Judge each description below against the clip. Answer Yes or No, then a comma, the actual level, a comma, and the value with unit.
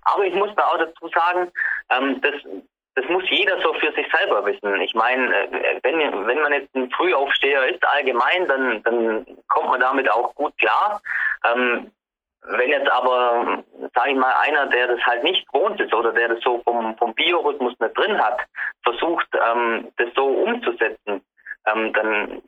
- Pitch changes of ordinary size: No, wide, 6.7 semitones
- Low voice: Yes, low, 125 Hz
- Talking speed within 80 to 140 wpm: No, average, 165 wpm